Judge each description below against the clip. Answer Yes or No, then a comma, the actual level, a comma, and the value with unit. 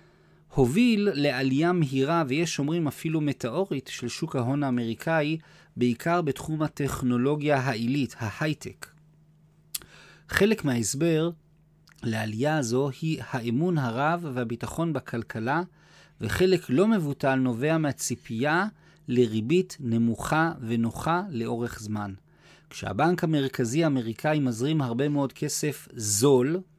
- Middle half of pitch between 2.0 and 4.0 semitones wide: No, average, 4.5 semitones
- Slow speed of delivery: Yes, slow, 95 wpm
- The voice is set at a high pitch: No, medium, 145 Hz